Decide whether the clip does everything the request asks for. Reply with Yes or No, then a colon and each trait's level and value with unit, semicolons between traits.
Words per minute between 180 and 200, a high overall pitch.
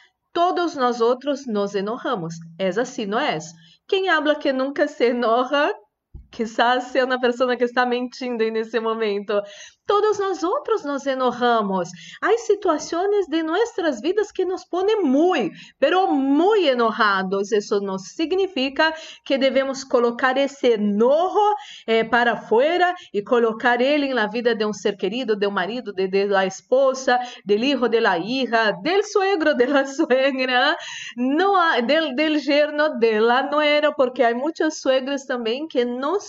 No: average, 150 wpm; very high, 260 Hz